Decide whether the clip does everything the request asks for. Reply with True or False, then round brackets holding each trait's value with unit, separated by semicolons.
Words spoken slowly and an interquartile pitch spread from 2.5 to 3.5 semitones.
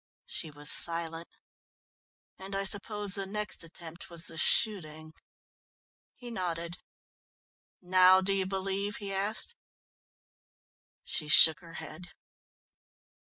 True (110 wpm; 3.0 semitones)